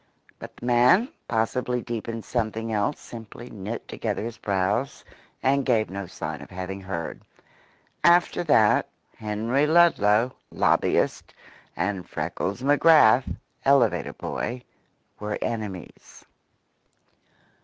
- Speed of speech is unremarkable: No, slow, 110 wpm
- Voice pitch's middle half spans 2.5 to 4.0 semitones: Yes, average, 3.6 semitones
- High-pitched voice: No, low, 115 Hz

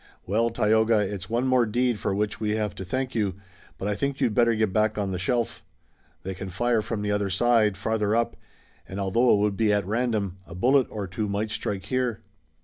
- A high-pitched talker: No, low, 105 Hz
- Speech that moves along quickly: Yes, fast, 220 wpm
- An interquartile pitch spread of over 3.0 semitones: No, average, 2.7 semitones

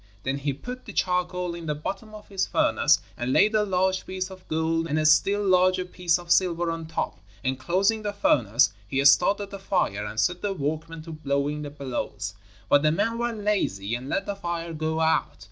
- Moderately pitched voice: Yes, medium, 170 Hz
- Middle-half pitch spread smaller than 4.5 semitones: No, average, 5.0 semitones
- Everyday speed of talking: No, fast, 210 wpm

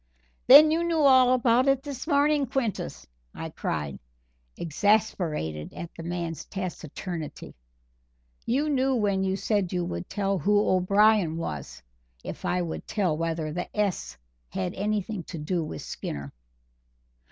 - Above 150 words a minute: No, average, 140 wpm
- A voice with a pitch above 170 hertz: Yes, high, 190 Hz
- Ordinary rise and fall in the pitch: No, wide, 6.9 semitones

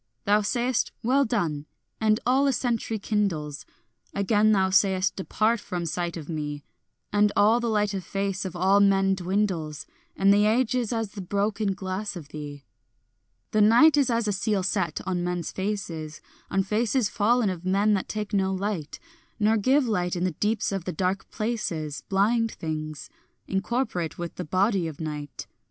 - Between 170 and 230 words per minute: Yes, average, 175 wpm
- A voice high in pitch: Yes, high, 200 Hz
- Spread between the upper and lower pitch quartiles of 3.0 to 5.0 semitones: Yes, average, 3.4 semitones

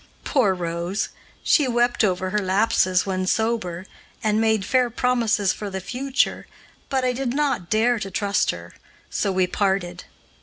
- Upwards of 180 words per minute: No, average, 155 wpm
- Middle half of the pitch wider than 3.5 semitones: Yes, average, 4.5 semitones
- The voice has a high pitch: Yes, high, 210 Hz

